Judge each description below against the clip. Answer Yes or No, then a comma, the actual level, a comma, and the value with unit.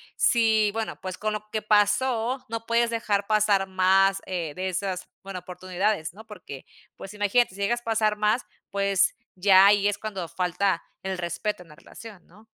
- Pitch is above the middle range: Yes, high, 200 Hz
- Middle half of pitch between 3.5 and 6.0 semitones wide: No, narrow, 2.5 semitones